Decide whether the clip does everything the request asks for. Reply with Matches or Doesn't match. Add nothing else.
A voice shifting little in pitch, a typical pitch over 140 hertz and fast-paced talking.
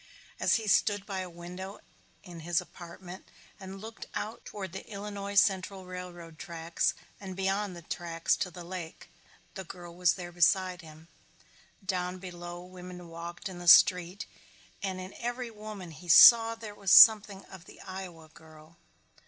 Doesn't match